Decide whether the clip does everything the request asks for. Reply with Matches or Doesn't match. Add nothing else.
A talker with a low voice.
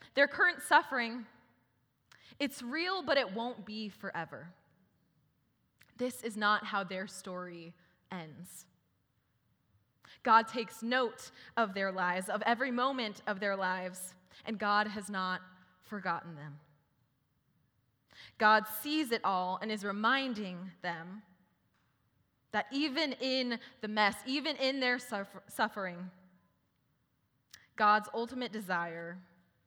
Doesn't match